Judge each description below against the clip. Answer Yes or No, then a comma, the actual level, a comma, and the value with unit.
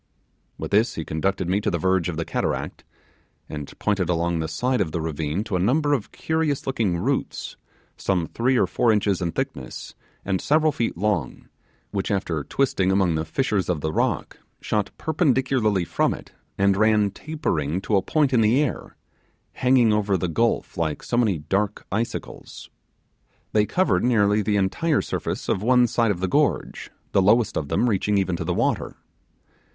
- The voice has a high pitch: No, low, 100 Hz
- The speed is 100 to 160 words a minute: No, average, 180 wpm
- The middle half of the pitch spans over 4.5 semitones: Yes, average, 5.2 semitones